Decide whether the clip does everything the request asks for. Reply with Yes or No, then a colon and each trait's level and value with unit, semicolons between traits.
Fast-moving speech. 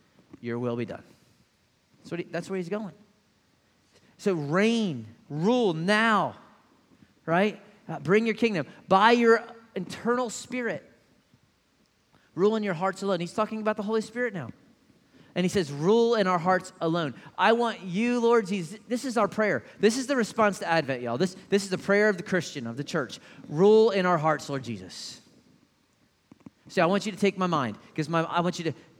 No: average, 185 wpm